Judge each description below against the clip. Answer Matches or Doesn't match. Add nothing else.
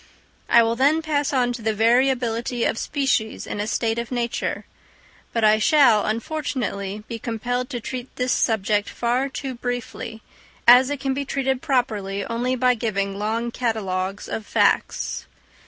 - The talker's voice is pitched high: Matches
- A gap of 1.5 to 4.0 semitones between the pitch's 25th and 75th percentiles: Matches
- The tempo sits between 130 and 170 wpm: Matches